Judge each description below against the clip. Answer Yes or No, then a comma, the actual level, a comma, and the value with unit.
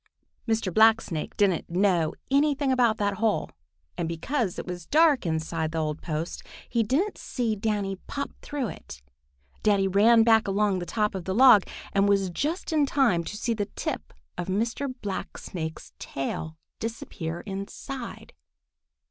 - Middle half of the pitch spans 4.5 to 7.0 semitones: Yes, average, 5.1 semitones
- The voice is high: Yes, high, 205 Hz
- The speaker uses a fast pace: No, average, 150 wpm